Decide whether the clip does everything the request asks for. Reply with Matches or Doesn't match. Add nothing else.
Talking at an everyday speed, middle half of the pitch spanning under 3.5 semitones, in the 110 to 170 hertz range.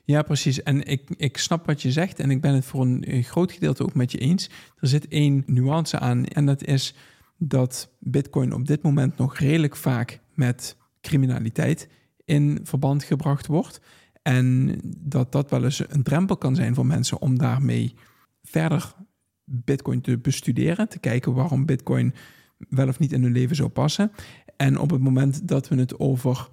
Matches